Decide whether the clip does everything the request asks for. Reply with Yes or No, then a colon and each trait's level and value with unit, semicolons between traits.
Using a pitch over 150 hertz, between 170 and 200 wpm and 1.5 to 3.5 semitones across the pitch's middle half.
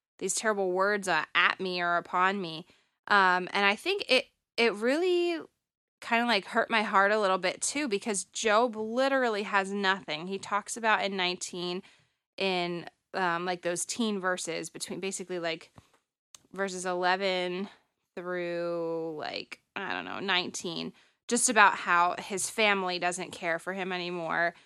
No: high, 190 Hz; average, 150 wpm; average, 2.9 semitones